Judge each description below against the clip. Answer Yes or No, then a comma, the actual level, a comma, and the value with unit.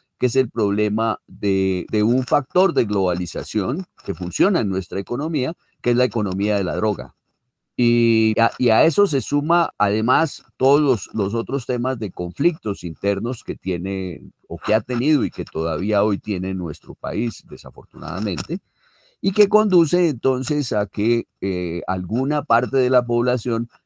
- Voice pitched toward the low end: Yes, low, 115 Hz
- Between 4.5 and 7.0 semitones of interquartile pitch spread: Yes, average, 5.1 semitones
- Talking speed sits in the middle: Yes, average, 160 wpm